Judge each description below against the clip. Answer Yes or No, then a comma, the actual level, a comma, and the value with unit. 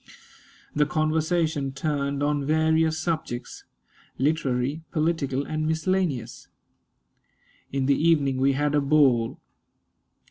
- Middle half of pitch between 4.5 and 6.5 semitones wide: No, narrow, 2.5 semitones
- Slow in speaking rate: Yes, slow, 100 wpm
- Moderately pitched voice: Yes, medium, 150 Hz